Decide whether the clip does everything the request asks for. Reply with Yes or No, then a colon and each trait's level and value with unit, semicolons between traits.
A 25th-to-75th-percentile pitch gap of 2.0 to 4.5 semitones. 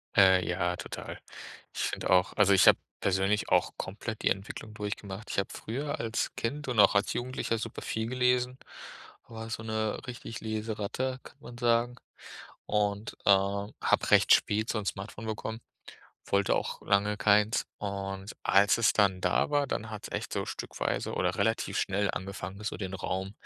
Yes: narrow, 2.5 semitones